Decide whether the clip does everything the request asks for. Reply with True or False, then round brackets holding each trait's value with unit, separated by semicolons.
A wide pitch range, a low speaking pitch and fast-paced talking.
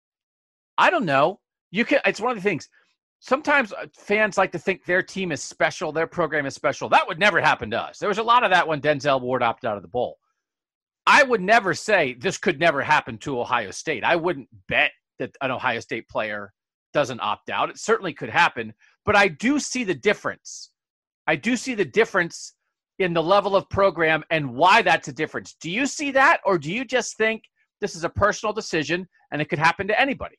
False (5.8 semitones; 185 Hz; 215 wpm)